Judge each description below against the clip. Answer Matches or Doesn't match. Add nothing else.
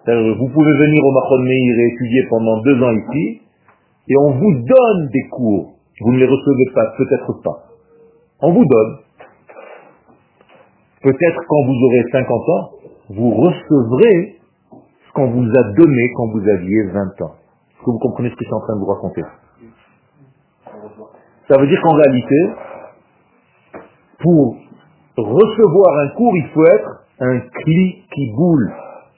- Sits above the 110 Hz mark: Matches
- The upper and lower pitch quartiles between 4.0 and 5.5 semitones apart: Matches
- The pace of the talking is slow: Doesn't match